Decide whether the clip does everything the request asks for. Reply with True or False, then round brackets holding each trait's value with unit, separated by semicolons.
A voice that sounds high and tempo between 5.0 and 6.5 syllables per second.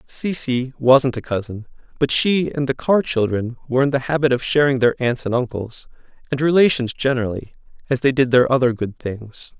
False (130 Hz; 5.2 syllables/s)